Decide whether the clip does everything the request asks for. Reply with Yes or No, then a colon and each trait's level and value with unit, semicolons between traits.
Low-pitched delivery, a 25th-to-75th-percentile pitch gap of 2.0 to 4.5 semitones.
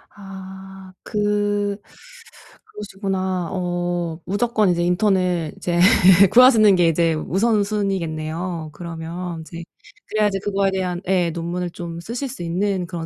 No: medium, 185 Hz; average, 2.8 semitones